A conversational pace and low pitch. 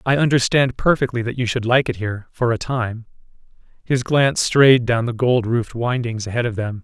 Yes: average, 195 wpm; low, 120 Hz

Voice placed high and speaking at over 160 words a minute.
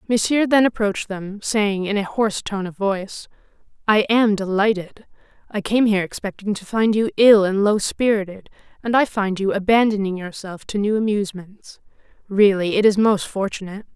Yes: high, 205 Hz; average, 170 wpm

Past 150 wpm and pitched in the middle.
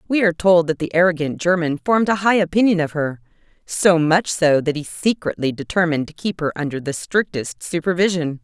Yes: average, 185 wpm; medium, 170 Hz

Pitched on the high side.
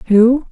Yes: high, 240 Hz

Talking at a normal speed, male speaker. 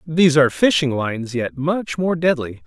Yes: average, 180 wpm; male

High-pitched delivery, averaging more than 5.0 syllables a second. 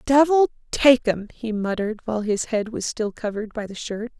Yes: high, 230 Hz; 5.5 syllables/s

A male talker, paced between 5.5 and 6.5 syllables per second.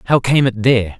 Yes: male; 6.2 syllables/s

